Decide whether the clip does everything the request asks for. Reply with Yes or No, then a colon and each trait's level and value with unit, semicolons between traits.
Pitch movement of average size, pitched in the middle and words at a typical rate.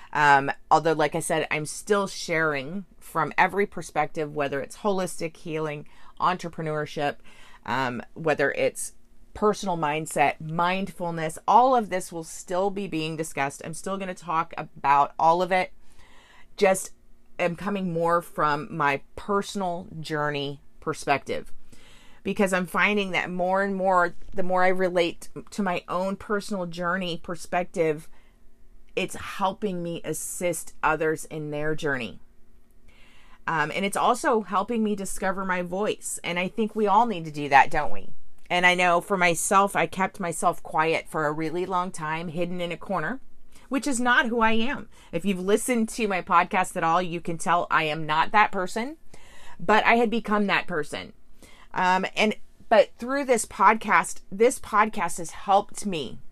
Yes: average, 3.9 semitones; medium, 180 Hz; average, 160 wpm